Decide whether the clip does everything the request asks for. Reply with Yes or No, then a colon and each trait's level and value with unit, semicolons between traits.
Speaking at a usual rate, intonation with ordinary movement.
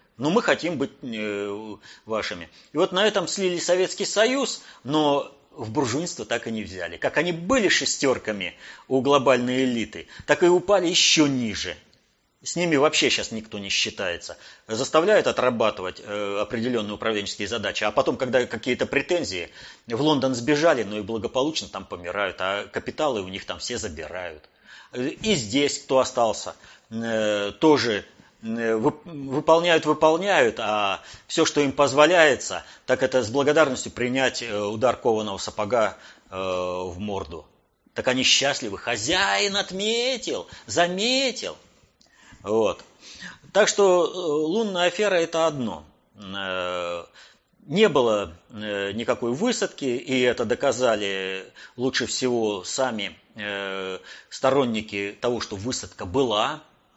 No: average, 120 wpm; wide, 6.9 semitones